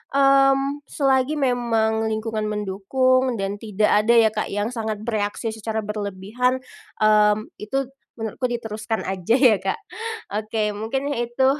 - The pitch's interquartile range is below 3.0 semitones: No, average, 3.3 semitones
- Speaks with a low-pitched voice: No, high, 220 Hz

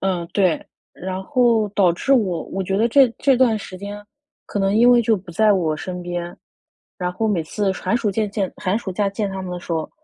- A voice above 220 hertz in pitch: No, high, 195 Hz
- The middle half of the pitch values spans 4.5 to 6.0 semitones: No, average, 3.3 semitones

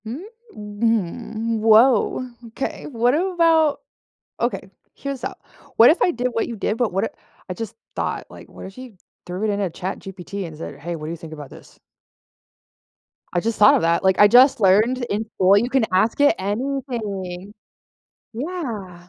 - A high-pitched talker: Yes, high, 220 Hz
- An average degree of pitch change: Yes, average, 4.9 semitones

